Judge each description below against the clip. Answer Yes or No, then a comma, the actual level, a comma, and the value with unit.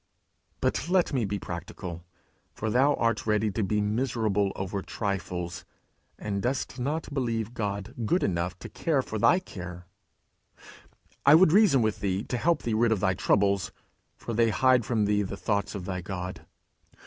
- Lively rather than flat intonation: No, average, 4.2 semitones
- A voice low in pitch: Yes, low, 105 Hz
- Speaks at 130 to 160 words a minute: No, average, 170 wpm